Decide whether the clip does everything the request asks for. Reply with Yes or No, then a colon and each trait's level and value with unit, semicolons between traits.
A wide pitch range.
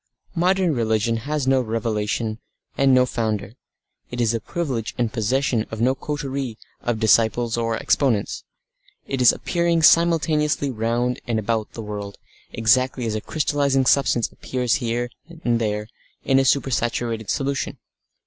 No: average, 3.4 semitones